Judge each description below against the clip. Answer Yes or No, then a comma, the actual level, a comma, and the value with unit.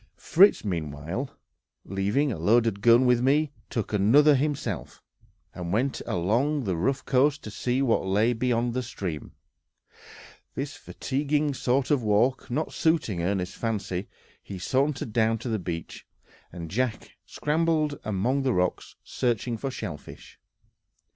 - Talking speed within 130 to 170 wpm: Yes, slow, 135 wpm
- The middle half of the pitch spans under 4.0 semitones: No, wide, 5.6 semitones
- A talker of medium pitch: No, low, 120 Hz